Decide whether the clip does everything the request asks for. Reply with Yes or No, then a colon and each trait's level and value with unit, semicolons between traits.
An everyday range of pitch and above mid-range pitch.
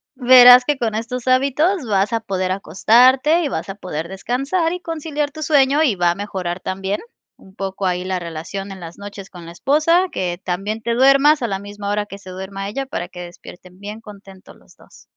No: wide, 5.9 semitones; high, 205 Hz